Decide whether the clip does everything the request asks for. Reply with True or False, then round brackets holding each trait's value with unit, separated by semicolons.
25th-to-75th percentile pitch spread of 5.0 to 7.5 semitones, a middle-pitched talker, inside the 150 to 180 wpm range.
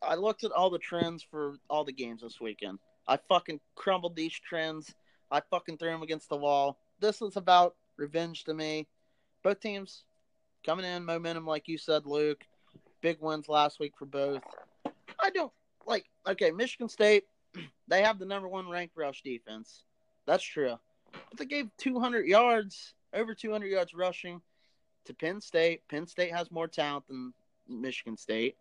False (4.5 semitones; 165 Hz; 170 wpm)